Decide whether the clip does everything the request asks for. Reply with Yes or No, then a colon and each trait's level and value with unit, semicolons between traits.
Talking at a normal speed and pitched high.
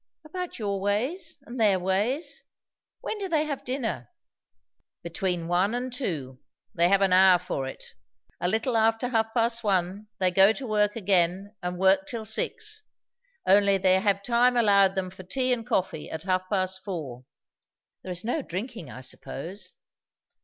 Yes: average, 165 wpm; high, 200 Hz